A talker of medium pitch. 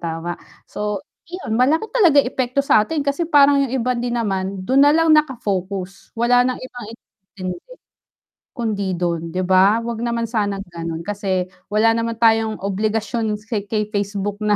No: high, 220 Hz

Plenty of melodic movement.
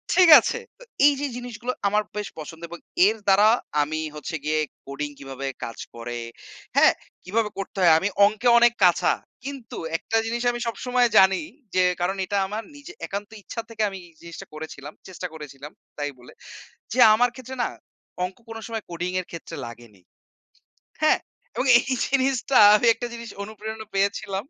Yes: wide, 6.2 semitones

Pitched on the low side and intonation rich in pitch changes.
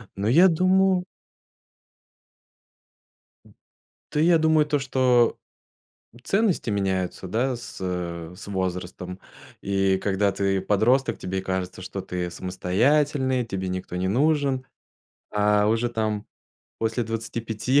Yes: low, 110 Hz; wide, 6.0 semitones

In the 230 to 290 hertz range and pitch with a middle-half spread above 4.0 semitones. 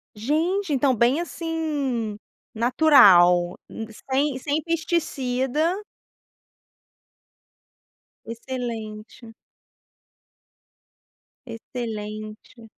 Yes: very high, 250 Hz; wide, 5.6 semitones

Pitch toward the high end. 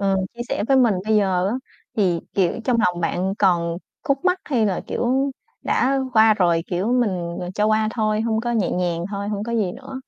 Yes: high, 210 Hz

